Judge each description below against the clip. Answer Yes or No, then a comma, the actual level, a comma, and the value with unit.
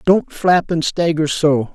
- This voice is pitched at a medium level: Yes, medium, 160 Hz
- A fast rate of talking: No, average, 170 wpm